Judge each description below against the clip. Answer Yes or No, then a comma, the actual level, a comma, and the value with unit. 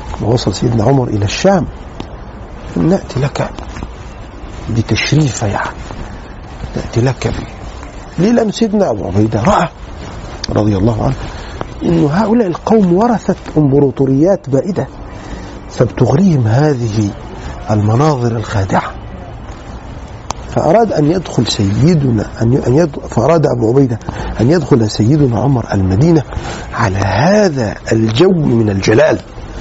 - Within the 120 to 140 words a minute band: No, average, 105 wpm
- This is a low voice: Yes, low, 120 Hz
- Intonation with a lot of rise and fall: Yes, wide, 6.2 semitones